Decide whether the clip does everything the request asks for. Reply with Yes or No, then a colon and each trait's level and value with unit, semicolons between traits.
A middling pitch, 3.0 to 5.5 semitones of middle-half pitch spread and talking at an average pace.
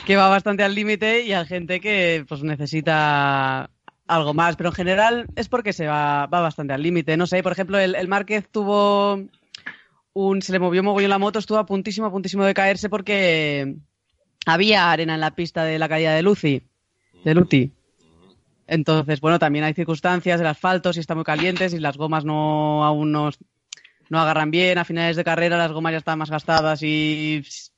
No: medium, 170 Hz; average, 4.1 semitones; fast, 200 wpm